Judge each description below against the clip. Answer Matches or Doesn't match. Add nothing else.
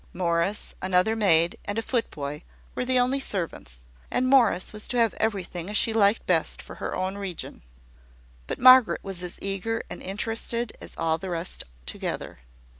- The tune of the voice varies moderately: Matches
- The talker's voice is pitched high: Matches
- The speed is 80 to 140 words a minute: Doesn't match